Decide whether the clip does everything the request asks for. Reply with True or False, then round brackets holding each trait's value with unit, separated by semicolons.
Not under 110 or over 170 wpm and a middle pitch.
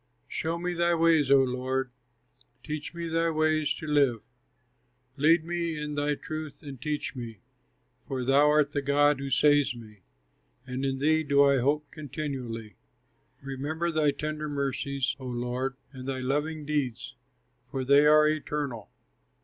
True (150 wpm; 145 Hz)